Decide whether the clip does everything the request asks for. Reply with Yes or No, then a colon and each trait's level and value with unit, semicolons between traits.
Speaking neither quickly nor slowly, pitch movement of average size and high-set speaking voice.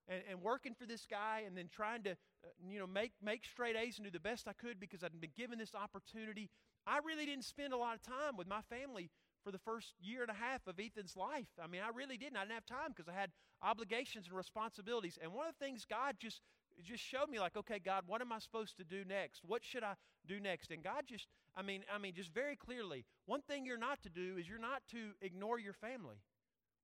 No: fast, 255 wpm; average, 3.9 semitones; high, 215 Hz